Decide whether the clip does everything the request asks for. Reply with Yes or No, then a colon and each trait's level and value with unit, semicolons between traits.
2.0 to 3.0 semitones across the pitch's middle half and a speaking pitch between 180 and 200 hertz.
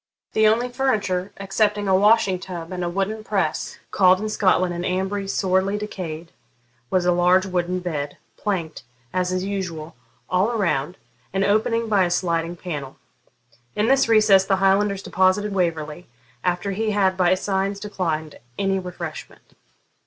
Yes: narrow, 2.5 semitones; high, 190 Hz